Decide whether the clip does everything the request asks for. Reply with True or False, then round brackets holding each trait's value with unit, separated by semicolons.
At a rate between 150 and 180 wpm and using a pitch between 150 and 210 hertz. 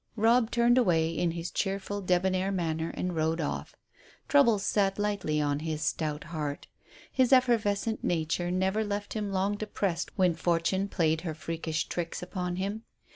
True (155 wpm; 185 Hz)